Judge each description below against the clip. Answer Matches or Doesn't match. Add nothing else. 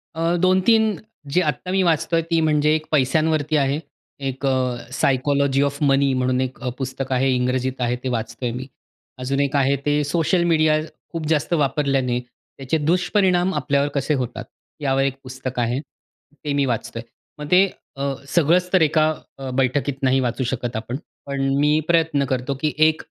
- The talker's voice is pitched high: Doesn't match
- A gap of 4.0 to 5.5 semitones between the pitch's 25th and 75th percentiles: Doesn't match